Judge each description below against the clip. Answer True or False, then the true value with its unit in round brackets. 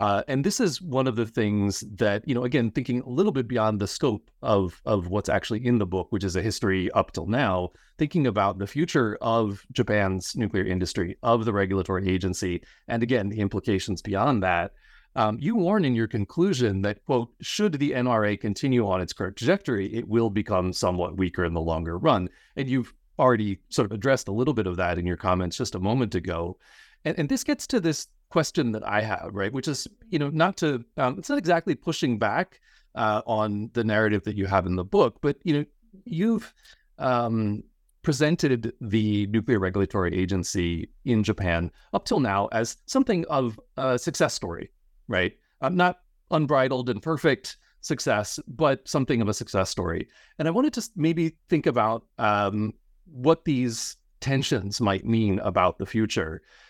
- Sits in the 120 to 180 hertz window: False (110 Hz)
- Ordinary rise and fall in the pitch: False (5.8 semitones)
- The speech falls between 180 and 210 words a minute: True (185 wpm)